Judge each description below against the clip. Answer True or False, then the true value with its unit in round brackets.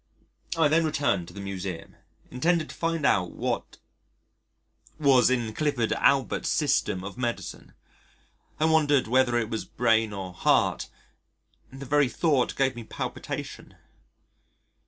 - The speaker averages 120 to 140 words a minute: True (135 wpm)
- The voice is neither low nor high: False (125 Hz)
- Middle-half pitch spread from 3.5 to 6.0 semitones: True (5.1 semitones)